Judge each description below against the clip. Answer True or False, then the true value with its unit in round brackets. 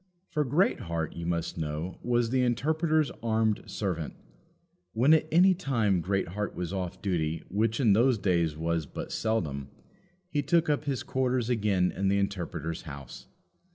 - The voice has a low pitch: True (100 Hz)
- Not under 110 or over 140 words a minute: False (155 wpm)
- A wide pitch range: True (7.1 semitones)